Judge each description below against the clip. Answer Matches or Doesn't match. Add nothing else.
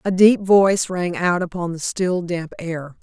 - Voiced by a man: Doesn't match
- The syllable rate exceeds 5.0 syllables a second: Doesn't match